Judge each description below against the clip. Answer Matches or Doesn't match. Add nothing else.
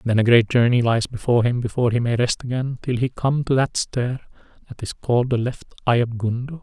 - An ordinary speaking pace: Doesn't match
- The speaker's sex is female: Doesn't match